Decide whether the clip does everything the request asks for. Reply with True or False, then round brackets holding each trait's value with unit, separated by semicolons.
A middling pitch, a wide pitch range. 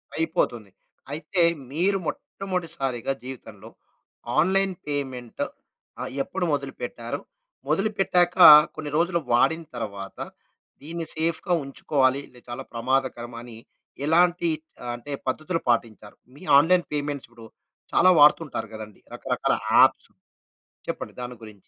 True (145 Hz; 5.8 semitones)